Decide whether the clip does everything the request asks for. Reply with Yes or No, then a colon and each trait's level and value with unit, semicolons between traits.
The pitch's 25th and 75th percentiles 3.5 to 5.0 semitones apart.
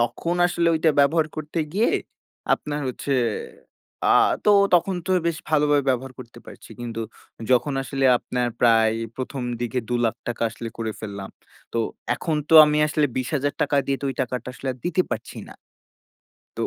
Yes: average, 4.1 semitones